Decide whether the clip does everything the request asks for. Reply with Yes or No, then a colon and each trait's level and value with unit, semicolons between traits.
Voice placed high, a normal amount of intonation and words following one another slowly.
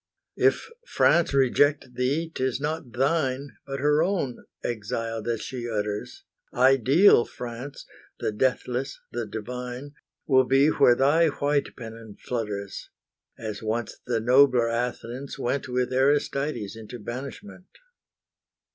No: low, 125 Hz; average, 3.3 semitones; slow, 120 wpm